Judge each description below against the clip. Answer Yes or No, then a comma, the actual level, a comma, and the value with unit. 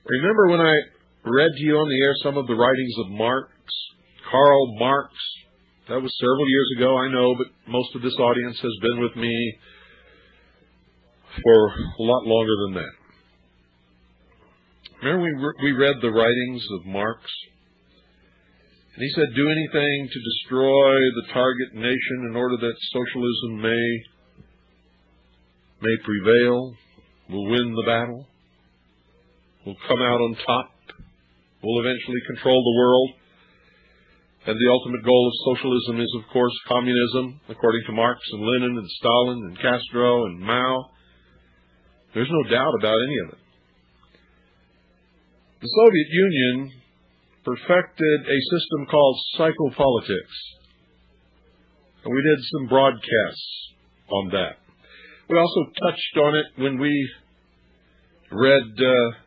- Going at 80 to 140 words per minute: Yes, slow, 135 wpm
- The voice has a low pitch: Yes, low, 120 Hz